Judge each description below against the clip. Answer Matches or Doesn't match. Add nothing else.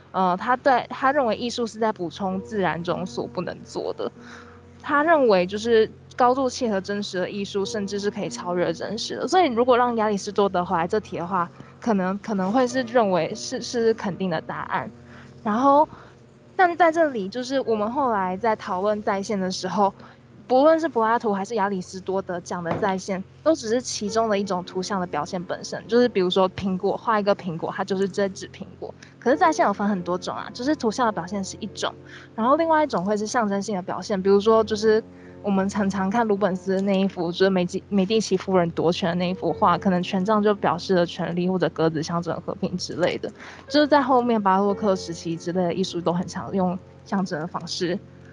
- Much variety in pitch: Doesn't match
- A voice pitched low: Doesn't match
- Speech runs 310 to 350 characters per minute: Matches